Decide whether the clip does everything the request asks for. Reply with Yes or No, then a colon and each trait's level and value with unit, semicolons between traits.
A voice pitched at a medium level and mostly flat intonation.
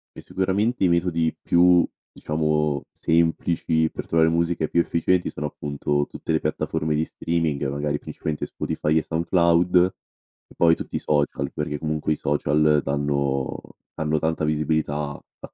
No: very low, 80 Hz; narrow, 2.1 semitones